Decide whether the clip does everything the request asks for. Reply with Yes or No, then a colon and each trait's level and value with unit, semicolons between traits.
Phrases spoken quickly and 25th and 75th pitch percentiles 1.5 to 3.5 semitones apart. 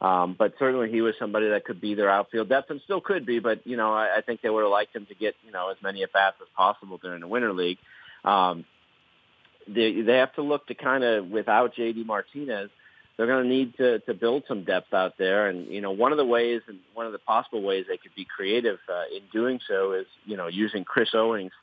No: fast, 245 wpm; average, 4.0 semitones